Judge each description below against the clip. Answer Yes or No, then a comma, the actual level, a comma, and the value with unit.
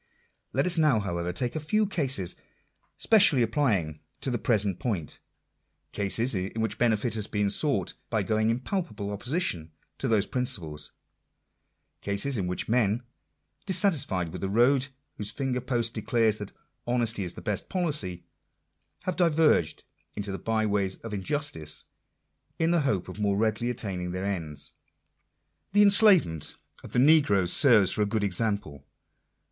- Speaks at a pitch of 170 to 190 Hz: No, low, 110 Hz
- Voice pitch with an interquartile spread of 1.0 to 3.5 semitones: No, wide, 5.6 semitones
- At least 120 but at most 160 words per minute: Yes, average, 155 wpm